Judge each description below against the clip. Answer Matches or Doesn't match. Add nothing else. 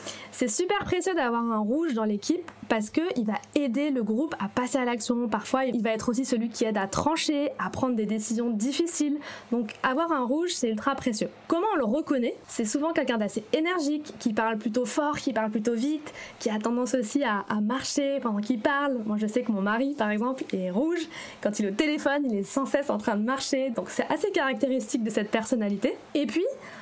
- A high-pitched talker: Matches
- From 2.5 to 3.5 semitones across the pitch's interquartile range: Doesn't match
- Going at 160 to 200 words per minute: Doesn't match